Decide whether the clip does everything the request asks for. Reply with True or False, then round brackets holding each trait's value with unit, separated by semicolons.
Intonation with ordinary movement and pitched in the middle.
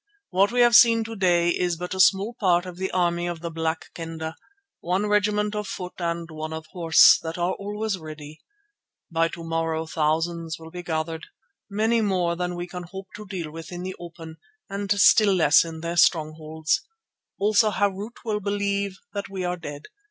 True (3.6 semitones; 175 Hz)